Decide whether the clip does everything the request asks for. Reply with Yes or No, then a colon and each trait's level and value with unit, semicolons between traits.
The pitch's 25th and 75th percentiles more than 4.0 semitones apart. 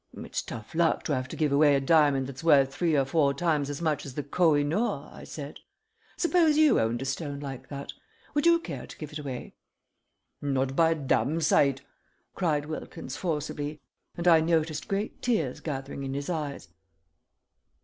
No: average, 3.1 semitones